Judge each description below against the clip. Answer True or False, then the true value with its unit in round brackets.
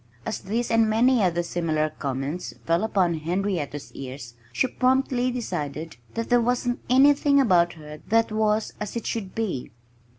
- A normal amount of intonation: False (7.1 semitones)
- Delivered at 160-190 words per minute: False (145 wpm)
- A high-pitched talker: True (210 Hz)